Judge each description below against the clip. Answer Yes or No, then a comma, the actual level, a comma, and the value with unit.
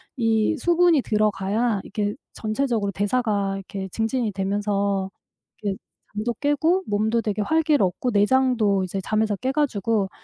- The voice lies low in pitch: No, high, 215 Hz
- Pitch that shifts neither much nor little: Yes, average, 3.9 semitones